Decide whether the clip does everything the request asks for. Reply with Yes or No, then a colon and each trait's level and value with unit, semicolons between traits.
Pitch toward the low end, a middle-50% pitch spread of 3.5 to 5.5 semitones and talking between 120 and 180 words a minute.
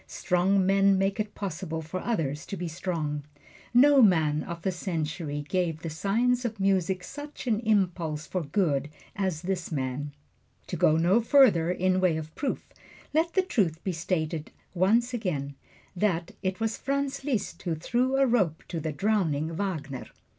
No: medium, 185 Hz; average, 5.0 semitones; average, 170 wpm